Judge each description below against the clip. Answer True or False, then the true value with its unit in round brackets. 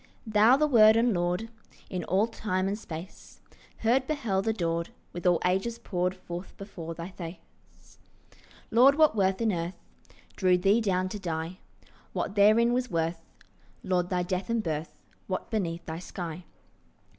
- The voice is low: False (190 Hz)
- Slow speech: False (155 wpm)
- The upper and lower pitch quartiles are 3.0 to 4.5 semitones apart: True (4.0 semitones)